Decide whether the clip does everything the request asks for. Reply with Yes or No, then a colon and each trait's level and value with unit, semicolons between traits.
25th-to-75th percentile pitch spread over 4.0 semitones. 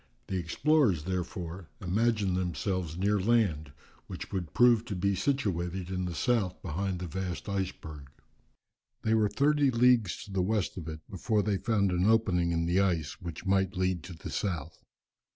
No: average, 3.4 semitones